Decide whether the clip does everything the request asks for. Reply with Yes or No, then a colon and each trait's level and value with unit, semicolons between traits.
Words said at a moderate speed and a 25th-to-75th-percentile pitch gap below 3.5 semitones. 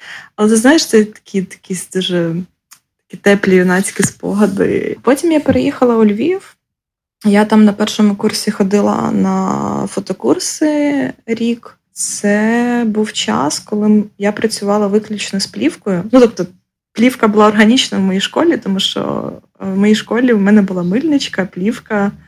Yes: average, 140 wpm; average, 2.9 semitones